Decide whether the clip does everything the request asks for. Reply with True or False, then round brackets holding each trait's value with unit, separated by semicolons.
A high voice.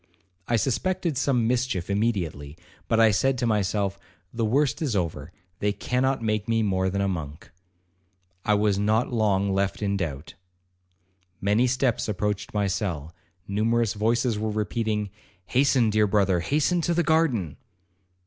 False (105 Hz)